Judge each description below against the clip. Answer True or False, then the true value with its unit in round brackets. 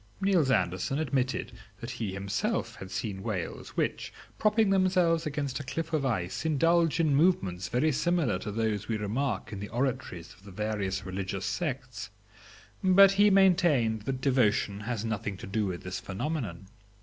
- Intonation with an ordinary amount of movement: False (8.0 semitones)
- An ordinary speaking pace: True (160 wpm)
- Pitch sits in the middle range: False (120 Hz)